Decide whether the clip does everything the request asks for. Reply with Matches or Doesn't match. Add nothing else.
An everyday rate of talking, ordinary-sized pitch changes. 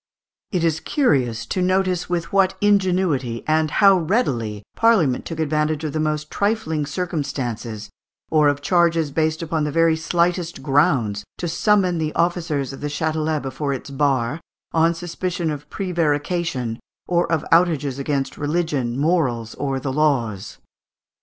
Matches